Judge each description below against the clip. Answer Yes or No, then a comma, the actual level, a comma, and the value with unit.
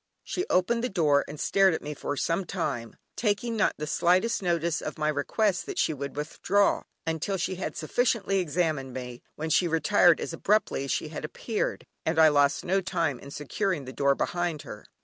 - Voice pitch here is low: No, medium, 165 Hz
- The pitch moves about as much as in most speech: Yes, average, 4.7 semitones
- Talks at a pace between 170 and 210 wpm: Yes, average, 195 wpm